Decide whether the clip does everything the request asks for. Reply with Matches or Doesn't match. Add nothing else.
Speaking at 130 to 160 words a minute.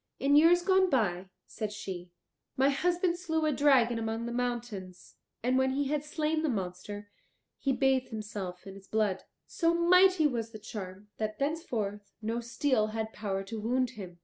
Doesn't match